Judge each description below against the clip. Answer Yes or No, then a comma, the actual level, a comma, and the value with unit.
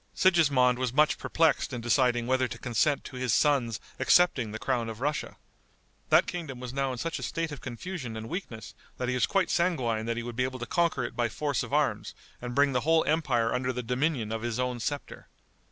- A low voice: Yes, low, 125 Hz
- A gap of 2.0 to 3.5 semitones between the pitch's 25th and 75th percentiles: No, average, 3.9 semitones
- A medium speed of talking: No, fast, 220 wpm